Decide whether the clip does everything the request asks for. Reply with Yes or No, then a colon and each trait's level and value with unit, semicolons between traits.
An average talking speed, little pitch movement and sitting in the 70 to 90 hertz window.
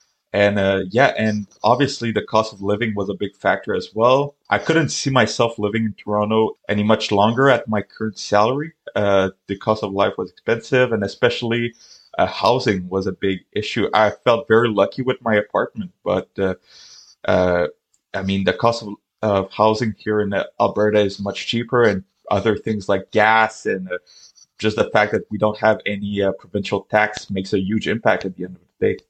No: average, 195 wpm; narrow, 2.3 semitones; low, 105 Hz